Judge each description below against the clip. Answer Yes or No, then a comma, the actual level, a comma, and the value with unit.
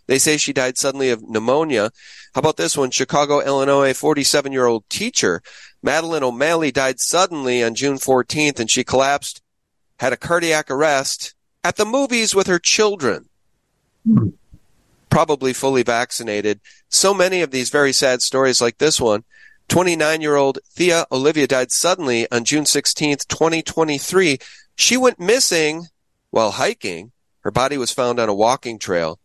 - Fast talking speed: No, average, 150 wpm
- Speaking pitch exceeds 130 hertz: Yes, medium, 140 Hz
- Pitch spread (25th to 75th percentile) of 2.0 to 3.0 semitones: No, average, 4.3 semitones